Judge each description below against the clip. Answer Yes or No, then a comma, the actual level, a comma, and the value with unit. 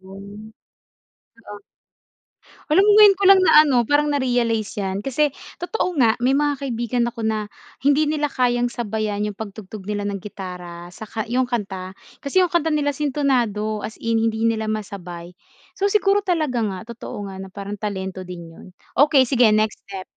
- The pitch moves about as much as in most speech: No, wide, 5.9 semitones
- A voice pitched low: No, high, 225 Hz